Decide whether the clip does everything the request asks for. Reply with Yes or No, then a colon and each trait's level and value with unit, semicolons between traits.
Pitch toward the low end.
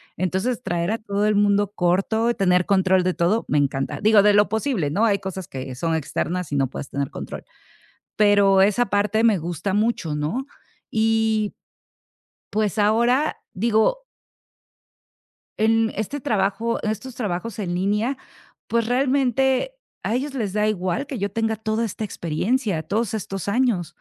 No: high, 210 Hz